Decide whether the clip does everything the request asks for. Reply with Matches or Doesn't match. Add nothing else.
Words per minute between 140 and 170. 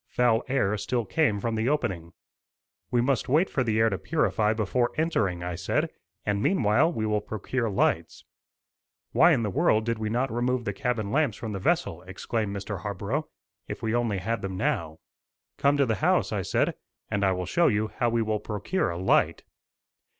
Doesn't match